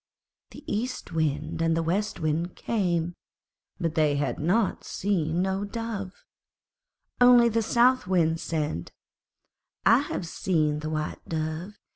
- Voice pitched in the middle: Yes, medium, 170 Hz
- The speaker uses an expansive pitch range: No, average, 4.5 semitones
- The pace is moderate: No, slow, 125 wpm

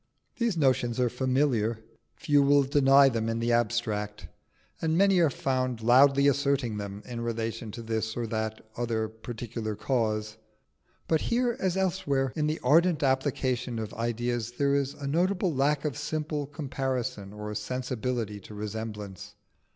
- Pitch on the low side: Yes, low, 125 Hz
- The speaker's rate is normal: Yes, average, 150 wpm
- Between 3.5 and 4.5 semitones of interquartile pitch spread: Yes, average, 4.2 semitones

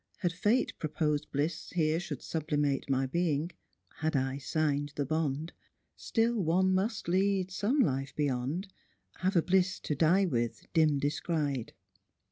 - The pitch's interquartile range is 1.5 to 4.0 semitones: No, average, 4.5 semitones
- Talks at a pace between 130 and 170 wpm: Yes, average, 150 wpm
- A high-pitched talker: No, medium, 155 Hz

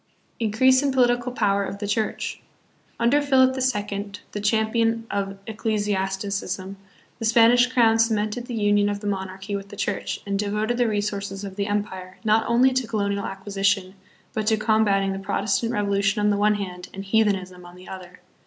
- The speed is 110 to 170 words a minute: No, average, 180 wpm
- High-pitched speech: Yes, high, 205 Hz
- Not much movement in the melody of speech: Yes, narrow, 2.3 semitones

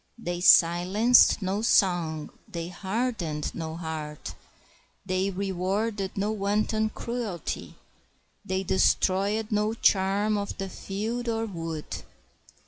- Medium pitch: No, high, 195 Hz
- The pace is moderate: No, slow, 105 wpm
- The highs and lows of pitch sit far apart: No, average, 3.5 semitones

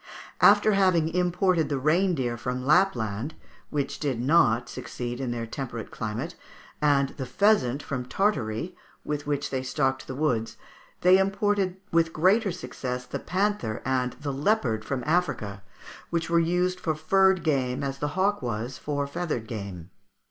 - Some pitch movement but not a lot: No, wide, 6.1 semitones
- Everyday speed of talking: Yes, average, 150 wpm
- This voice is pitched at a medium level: Yes, medium, 145 Hz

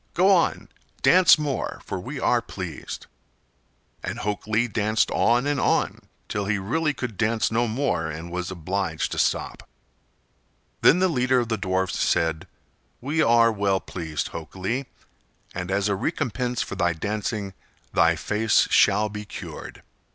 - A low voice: Yes, low, 105 Hz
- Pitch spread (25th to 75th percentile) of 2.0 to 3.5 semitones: No, average, 4.6 semitones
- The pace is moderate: Yes, average, 150 wpm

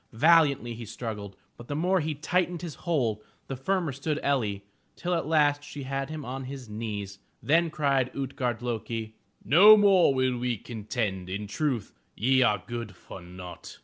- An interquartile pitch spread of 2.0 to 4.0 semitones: No, wide, 5.6 semitones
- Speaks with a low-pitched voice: Yes, low, 130 Hz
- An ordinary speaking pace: Yes, average, 170 wpm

